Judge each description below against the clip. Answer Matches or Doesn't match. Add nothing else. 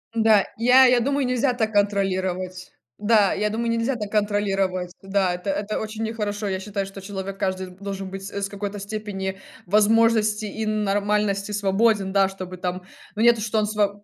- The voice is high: Matches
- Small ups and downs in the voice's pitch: Matches